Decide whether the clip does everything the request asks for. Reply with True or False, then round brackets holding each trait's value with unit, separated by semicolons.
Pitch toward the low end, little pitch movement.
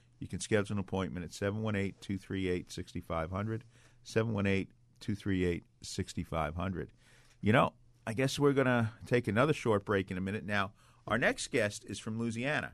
False (105 Hz; 3.9 semitones)